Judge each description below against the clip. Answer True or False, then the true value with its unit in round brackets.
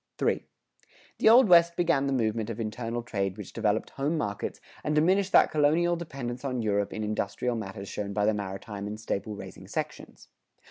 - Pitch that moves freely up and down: True (6.5 semitones)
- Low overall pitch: True (115 Hz)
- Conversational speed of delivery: True (180 wpm)